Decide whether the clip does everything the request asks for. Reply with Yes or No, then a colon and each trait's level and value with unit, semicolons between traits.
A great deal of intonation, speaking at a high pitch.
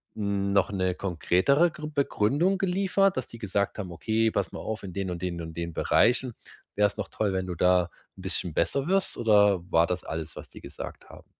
No: wide, 6.1 semitones; low, 100 Hz